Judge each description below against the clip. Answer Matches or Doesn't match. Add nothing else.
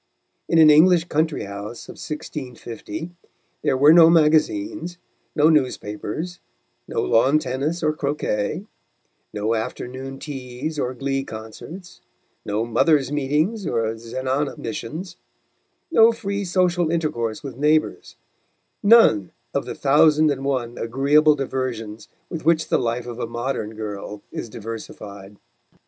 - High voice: Doesn't match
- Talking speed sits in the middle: Doesn't match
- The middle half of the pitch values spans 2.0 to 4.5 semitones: Doesn't match